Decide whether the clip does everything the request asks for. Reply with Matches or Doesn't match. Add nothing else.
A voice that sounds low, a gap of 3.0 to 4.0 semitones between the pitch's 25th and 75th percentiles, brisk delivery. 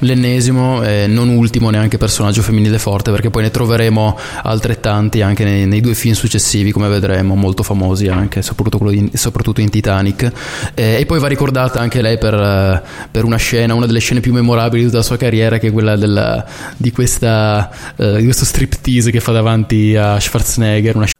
Doesn't match